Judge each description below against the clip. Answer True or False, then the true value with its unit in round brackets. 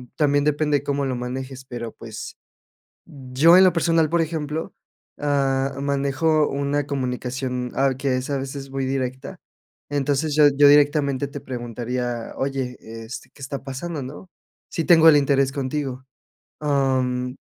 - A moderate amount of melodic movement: False (2.0 semitones)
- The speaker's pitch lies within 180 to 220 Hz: False (135 Hz)